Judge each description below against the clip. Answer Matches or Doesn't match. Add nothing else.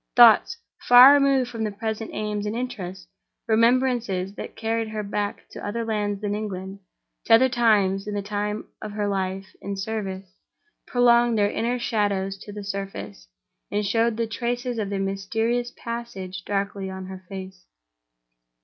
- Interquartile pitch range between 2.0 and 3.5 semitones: Matches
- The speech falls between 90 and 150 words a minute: Doesn't match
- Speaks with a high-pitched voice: Matches